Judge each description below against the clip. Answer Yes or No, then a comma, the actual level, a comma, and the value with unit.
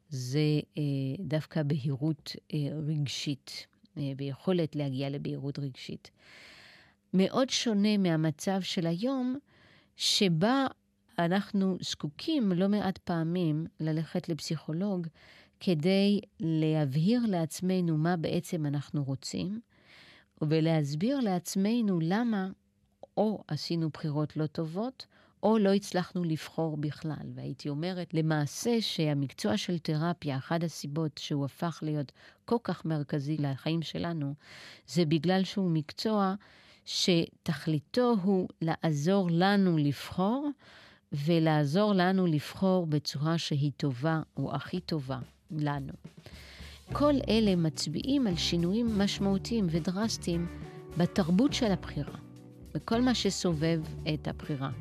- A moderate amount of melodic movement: Yes, average, 4.2 semitones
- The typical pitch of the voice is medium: Yes, medium, 165 Hz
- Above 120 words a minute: No, average, 105 wpm